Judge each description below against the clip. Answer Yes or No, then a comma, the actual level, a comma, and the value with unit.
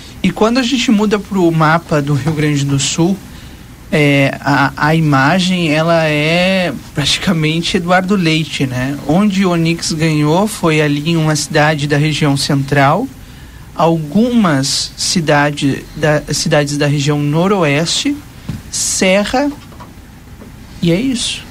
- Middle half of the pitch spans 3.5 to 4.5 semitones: Yes, average, 3.8 semitones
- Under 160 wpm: Yes, average, 125 wpm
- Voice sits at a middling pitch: Yes, medium, 160 Hz